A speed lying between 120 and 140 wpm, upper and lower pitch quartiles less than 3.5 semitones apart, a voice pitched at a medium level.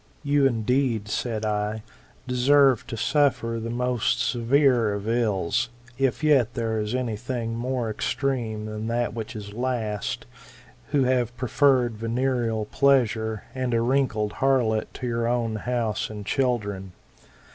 No: slow, 135 wpm; average, 2.8 semitones; low, 120 Hz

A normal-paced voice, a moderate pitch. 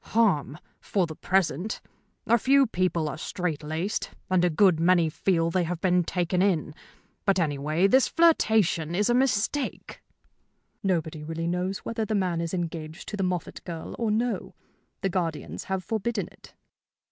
Yes: average, 160 wpm; medium, 180 Hz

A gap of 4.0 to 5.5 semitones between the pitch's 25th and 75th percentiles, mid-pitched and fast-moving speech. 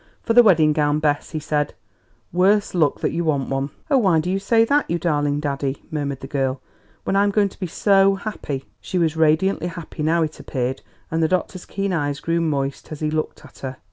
Yes: average, 4.5 semitones; medium, 160 Hz; fast, 220 wpm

